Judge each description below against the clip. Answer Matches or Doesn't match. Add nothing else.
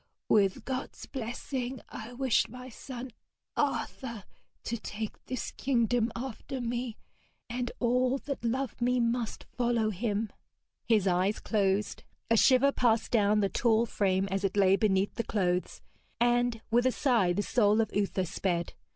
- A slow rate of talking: Doesn't match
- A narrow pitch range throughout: Doesn't match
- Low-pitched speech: Doesn't match